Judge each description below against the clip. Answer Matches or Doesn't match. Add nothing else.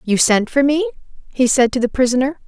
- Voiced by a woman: Matches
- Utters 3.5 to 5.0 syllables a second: Doesn't match